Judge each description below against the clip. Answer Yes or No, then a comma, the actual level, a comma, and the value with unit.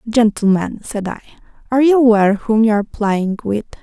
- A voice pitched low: No, high, 220 Hz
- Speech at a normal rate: Yes, average, 170 wpm